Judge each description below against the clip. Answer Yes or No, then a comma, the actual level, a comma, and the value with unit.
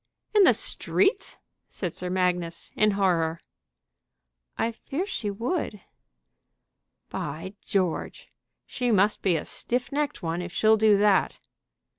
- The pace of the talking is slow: Yes, slow, 125 wpm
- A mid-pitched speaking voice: No, high, 200 Hz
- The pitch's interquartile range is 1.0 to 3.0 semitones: No, average, 4.6 semitones